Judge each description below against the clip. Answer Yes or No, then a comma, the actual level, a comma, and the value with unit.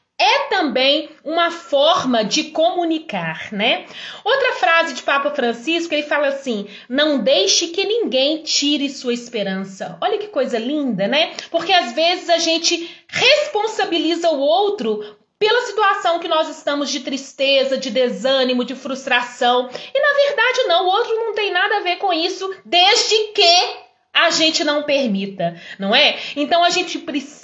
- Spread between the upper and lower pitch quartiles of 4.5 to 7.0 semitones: Yes, average, 4.9 semitones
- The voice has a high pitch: Yes, very high, 300 Hz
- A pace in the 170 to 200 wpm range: No, average, 155 wpm